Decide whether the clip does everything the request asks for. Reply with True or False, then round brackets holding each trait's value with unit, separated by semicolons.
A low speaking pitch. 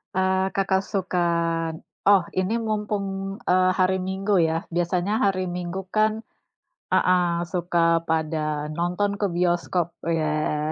False (180 Hz)